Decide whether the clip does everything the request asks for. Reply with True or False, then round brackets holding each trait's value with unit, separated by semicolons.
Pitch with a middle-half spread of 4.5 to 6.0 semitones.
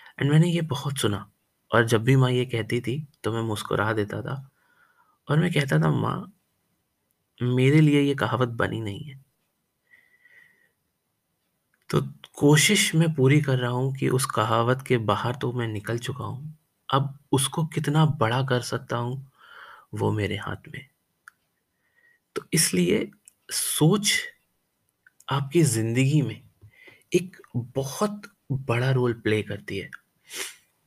True (4.8 semitones)